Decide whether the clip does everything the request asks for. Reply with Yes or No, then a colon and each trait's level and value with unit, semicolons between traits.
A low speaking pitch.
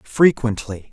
Yes: low, 120 Hz